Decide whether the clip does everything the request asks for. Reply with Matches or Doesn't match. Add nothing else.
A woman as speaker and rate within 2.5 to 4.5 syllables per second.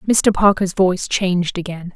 Doesn't match